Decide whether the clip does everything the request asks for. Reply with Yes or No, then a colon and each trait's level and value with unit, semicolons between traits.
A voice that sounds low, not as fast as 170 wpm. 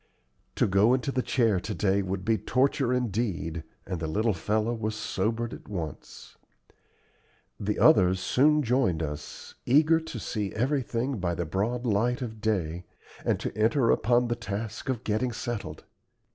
Yes: low, 110 Hz; average, 160 wpm